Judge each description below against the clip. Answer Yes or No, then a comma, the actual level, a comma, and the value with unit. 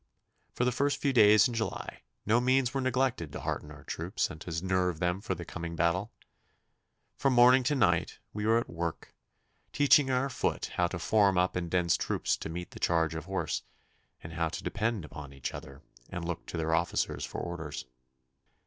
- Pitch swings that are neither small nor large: No, wide, 6.5 semitones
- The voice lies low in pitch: Yes, very low, 90 Hz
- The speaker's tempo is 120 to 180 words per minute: No, average, 195 wpm